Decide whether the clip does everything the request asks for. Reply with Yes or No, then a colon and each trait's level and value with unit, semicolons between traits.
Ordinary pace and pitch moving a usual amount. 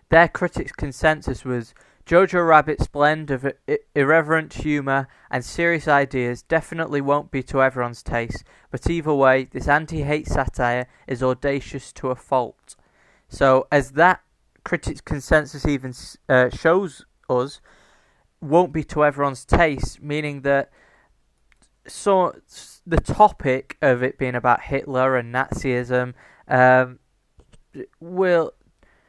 No: slow, 125 wpm; average, 3.5 semitones